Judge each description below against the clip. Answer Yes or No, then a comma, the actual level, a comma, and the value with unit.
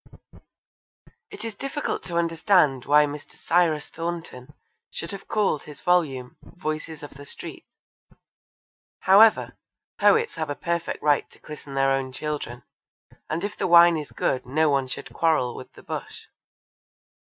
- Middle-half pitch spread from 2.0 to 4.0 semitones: Yes, average, 3.5 semitones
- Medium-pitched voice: Yes, medium, 155 Hz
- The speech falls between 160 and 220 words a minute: No, average, 145 wpm